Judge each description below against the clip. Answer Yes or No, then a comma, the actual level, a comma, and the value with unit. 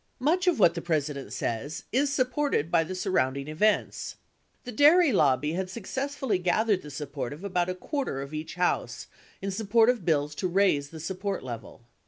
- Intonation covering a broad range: Yes, wide, 7.3 semitones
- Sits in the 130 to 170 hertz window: No, medium, 180 Hz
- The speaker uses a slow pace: No, average, 180 wpm